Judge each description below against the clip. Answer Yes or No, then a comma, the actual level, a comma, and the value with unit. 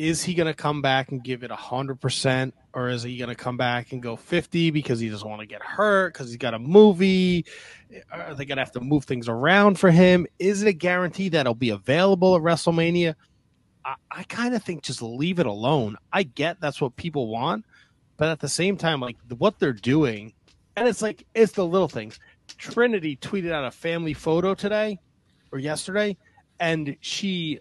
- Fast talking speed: Yes, fast, 210 wpm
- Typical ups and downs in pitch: No, wide, 6.2 semitones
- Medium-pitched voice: Yes, medium, 155 Hz